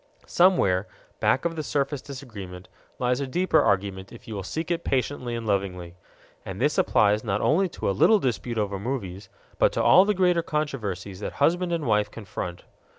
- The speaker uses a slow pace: No, average, 185 wpm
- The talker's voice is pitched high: No, low, 115 Hz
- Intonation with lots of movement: Yes, wide, 7.7 semitones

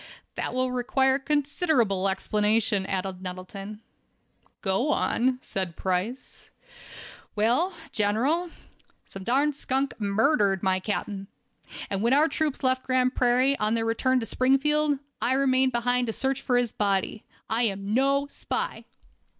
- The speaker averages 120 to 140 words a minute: Yes, slow, 135 wpm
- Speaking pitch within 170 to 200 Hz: No, high, 245 Hz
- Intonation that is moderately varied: Yes, average, 4.9 semitones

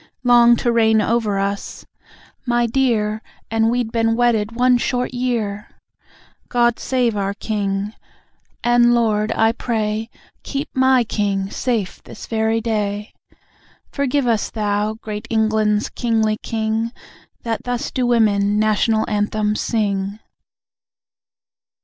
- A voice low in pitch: No, high, 225 Hz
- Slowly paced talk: Yes, slow, 120 wpm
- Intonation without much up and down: Yes, narrow, 2.2 semitones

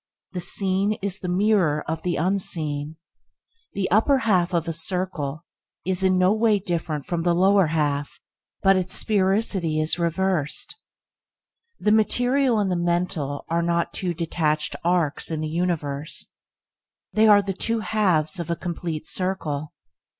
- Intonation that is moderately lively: Yes, average, 3.5 semitones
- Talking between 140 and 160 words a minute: Yes, average, 150 wpm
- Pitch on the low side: No, medium, 175 Hz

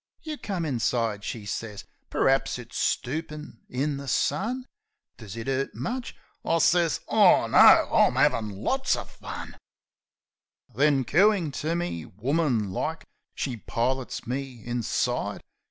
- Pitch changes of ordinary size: No, wide, 6.0 semitones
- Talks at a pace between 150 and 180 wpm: No, average, 140 wpm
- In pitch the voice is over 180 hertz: No, low, 135 Hz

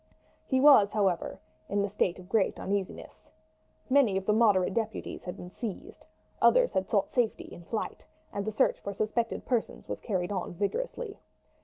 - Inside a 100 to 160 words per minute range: No, average, 170 wpm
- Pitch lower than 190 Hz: No, high, 205 Hz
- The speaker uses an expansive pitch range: No, average, 3.4 semitones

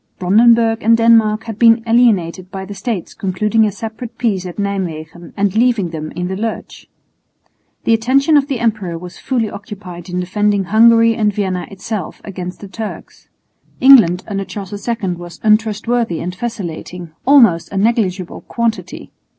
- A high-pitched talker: Yes, high, 205 Hz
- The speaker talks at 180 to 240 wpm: No, average, 155 wpm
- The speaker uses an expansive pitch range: No, average, 3.9 semitones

